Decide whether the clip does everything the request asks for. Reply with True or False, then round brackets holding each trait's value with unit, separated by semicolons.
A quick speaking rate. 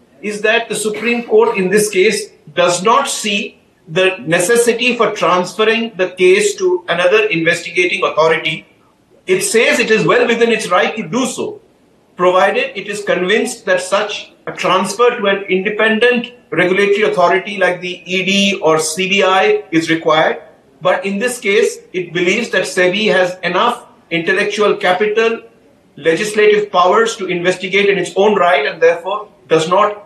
False (150 wpm)